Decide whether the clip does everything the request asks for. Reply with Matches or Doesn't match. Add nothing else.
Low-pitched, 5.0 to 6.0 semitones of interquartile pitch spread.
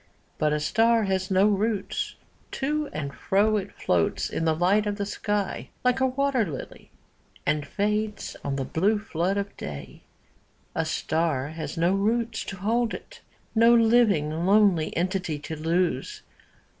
Doesn't match